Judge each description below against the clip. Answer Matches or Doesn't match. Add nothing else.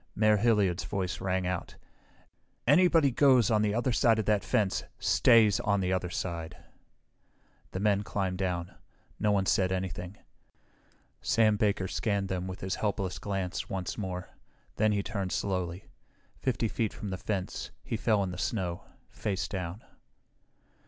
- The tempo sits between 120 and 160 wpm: Matches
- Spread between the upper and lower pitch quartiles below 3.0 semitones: Matches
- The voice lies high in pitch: Doesn't match